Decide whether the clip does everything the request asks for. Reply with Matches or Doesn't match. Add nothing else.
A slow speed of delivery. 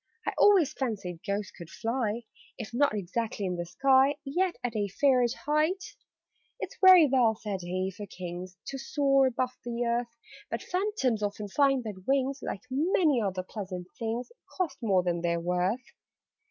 Doesn't match